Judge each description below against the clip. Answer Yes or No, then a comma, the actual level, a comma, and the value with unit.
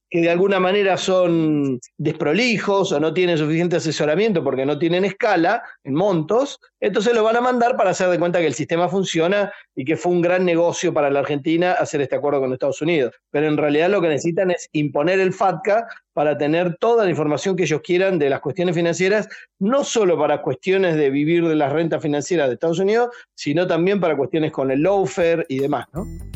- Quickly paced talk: Yes, fast, 205 wpm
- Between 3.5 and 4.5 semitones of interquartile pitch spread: Yes, average, 4.0 semitones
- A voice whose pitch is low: No, medium, 170 Hz